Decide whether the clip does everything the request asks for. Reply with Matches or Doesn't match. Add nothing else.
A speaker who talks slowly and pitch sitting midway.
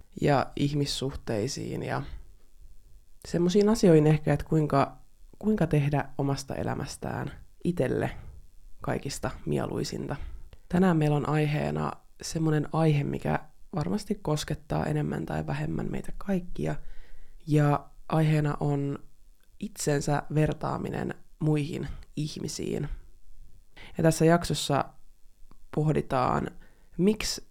Matches